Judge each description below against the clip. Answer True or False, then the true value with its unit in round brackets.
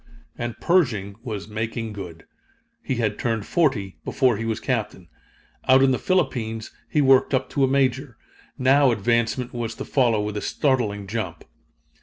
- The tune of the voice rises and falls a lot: False (3.7 semitones)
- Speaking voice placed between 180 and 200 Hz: False (115 Hz)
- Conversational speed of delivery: True (160 wpm)